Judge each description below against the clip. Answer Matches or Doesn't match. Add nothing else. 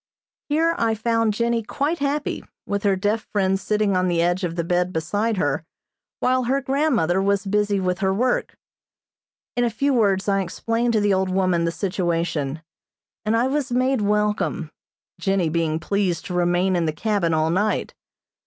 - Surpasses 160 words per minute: Matches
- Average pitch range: Matches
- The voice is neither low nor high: Doesn't match